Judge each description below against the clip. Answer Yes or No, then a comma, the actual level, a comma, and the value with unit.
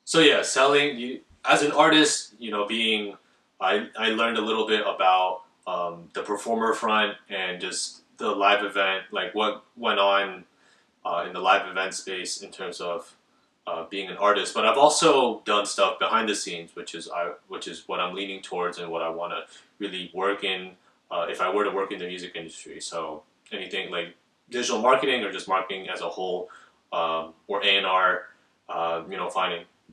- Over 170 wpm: Yes, average, 190 wpm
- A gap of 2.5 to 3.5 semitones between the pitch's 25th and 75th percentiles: Yes, average, 3.0 semitones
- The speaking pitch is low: Yes, low, 100 Hz